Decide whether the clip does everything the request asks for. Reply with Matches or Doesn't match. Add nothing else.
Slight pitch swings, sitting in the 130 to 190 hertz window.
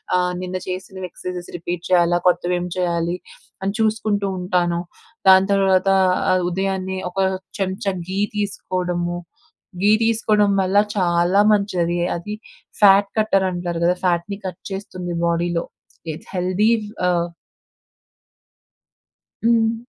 Matches